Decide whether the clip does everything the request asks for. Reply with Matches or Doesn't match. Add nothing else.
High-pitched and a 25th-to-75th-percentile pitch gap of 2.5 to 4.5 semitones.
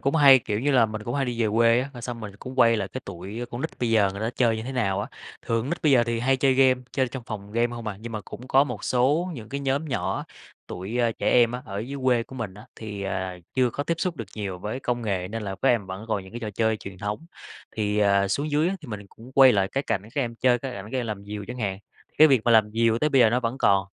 Doesn't match